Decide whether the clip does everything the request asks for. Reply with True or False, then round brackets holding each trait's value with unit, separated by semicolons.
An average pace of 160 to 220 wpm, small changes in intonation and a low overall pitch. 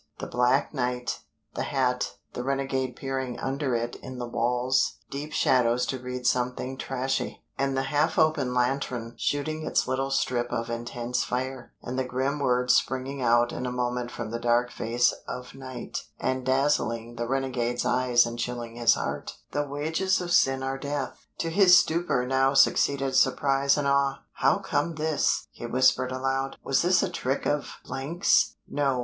True (170 wpm; 2.0 semitones; 130 Hz)